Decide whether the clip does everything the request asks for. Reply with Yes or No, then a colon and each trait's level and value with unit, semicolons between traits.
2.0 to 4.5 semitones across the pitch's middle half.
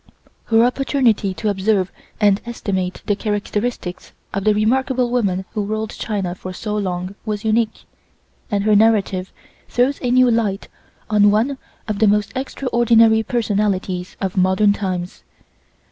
Yes: average, 2.9 semitones